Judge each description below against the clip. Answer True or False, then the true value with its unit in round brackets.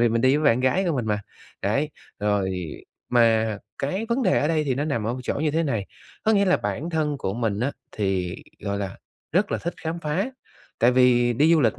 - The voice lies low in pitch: True (130 Hz)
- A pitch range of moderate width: False (6.1 semitones)